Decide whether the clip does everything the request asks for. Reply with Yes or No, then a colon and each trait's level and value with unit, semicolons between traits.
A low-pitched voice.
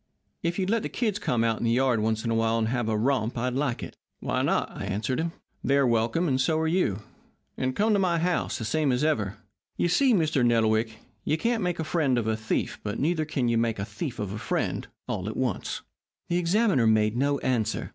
Yes: low, 125 Hz